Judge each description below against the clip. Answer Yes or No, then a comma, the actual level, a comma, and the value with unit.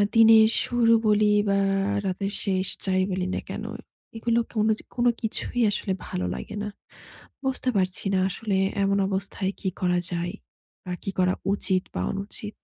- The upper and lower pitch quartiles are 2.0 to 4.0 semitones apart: Yes, average, 2.8 semitones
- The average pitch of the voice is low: No, high, 195 Hz